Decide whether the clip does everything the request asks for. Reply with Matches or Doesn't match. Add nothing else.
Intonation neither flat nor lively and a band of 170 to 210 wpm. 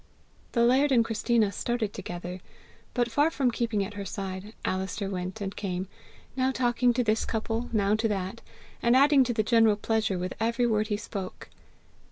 Matches